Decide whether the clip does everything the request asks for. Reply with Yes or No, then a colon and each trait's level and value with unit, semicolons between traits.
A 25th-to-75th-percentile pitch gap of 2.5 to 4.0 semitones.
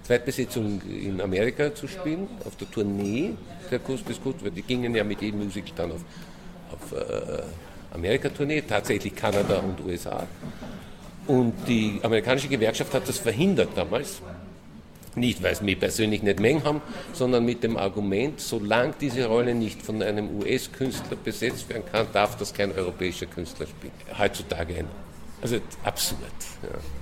No: average, 4.6 semitones